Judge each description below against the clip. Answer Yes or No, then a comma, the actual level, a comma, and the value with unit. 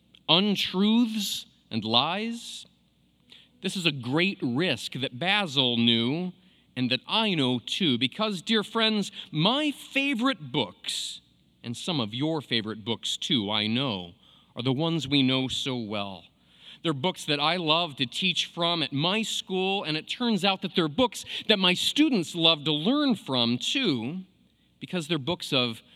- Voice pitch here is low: No, medium, 165 Hz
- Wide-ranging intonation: Yes, wide, 8.1 semitones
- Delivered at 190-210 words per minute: No, average, 155 wpm